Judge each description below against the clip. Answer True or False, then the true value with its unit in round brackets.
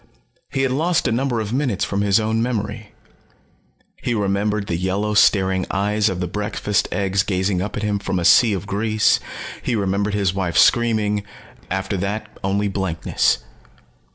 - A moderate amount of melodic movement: False (2.1 semitones)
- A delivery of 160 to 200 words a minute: True (165 wpm)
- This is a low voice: True (105 Hz)